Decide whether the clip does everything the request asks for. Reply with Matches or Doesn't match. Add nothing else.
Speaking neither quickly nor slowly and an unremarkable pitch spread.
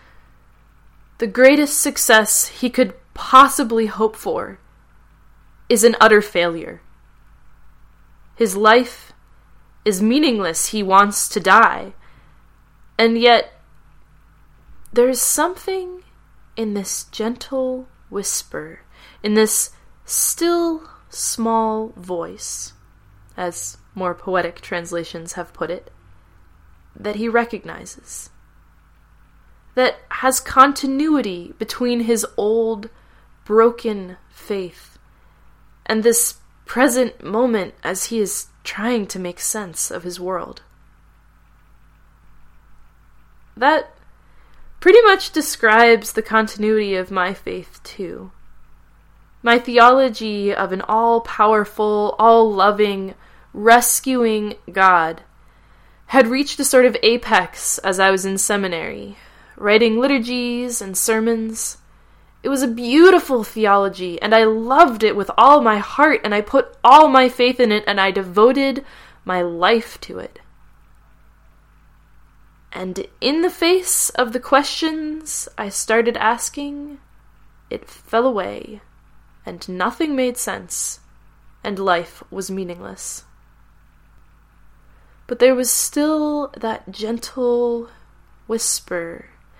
Doesn't match